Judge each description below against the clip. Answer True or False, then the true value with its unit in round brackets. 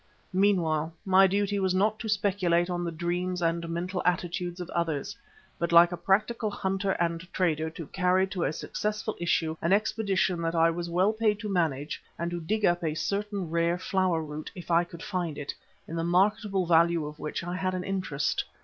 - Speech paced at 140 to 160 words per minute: False (195 wpm)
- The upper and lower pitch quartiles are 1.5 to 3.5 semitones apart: True (2.5 semitones)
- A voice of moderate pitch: True (175 Hz)